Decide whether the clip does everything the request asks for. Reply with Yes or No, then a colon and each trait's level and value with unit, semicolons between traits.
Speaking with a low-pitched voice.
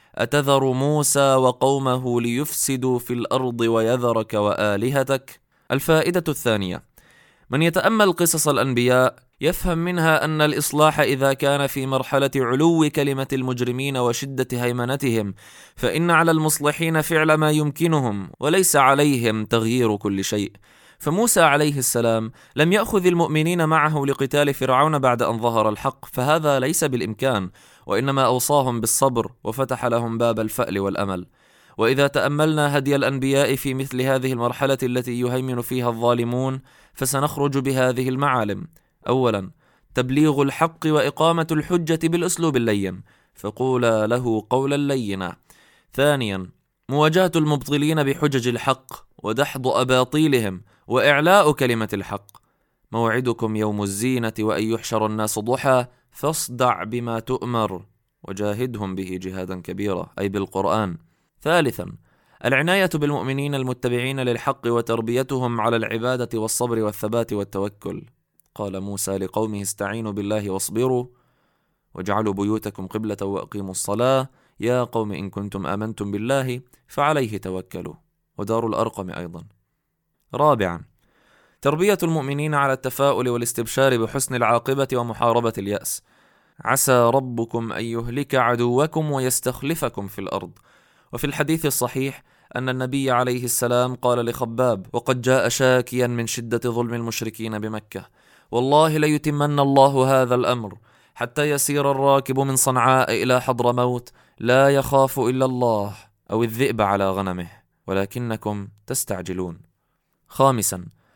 Yes: low, 125 Hz